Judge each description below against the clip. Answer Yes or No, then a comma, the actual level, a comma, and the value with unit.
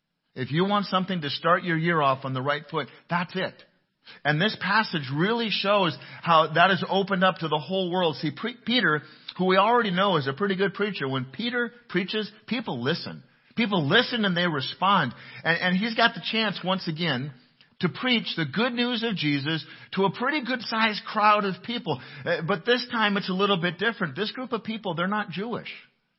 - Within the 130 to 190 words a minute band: No, average, 200 wpm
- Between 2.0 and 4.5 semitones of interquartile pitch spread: No, average, 4.9 semitones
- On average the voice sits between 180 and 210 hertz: Yes, high, 190 Hz